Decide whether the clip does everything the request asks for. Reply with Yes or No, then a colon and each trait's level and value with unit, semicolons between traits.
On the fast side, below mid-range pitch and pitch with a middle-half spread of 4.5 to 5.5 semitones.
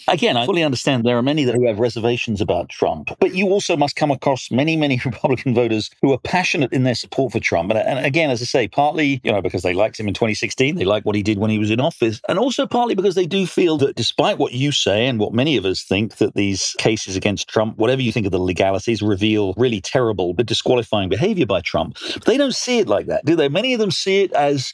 Yes: fast, 260 wpm; low, 120 Hz; average, 5.1 semitones